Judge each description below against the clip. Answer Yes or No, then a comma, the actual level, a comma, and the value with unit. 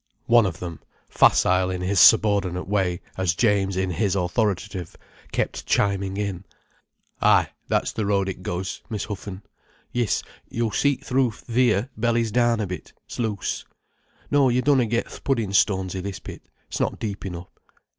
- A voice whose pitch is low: Yes, low, 100 Hz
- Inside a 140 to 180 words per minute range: Yes, average, 155 wpm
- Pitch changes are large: No, average, 3.7 semitones